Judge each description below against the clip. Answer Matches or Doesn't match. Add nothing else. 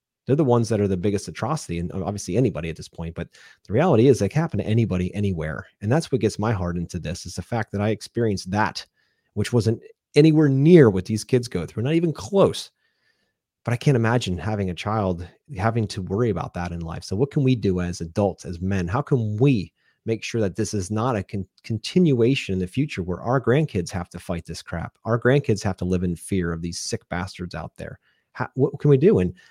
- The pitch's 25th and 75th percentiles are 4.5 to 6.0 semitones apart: Matches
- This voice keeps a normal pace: Doesn't match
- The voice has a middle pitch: Doesn't match